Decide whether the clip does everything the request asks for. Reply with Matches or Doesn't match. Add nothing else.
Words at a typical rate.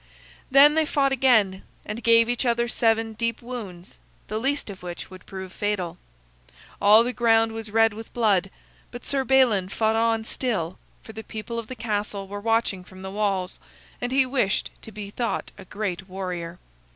Matches